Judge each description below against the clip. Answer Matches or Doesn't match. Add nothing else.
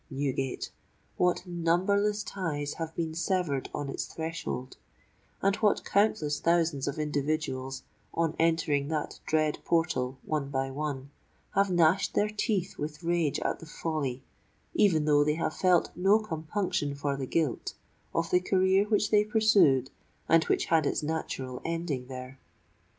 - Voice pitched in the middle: Matches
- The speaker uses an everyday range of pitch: Matches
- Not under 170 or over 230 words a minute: Doesn't match